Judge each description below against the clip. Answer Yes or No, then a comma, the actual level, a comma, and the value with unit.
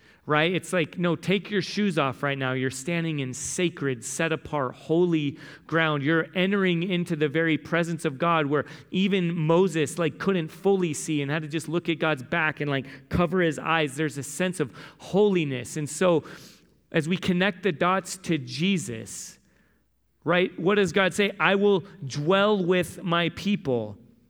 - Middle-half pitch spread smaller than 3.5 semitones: No, average, 3.8 semitones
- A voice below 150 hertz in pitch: No, medium, 165 Hz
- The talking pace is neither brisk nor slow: Yes, average, 175 wpm